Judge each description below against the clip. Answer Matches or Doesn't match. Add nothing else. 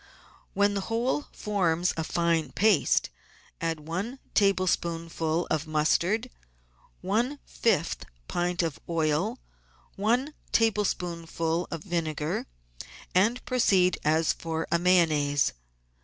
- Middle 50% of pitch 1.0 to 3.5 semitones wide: Doesn't match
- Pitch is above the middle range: Doesn't match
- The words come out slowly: Matches